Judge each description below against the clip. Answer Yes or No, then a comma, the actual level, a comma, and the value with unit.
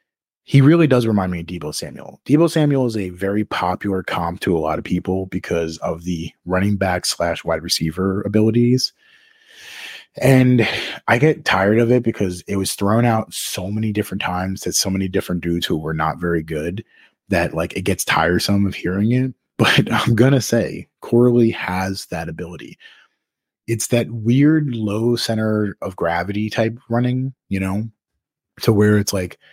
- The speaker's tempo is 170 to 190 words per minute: Yes, average, 175 wpm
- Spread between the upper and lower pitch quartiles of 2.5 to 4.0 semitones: No, average, 4.8 semitones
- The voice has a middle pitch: No, low, 105 Hz